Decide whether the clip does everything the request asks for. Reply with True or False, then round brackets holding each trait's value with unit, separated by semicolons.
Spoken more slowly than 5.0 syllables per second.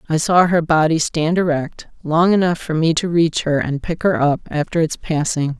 True (4.8 syllables/s)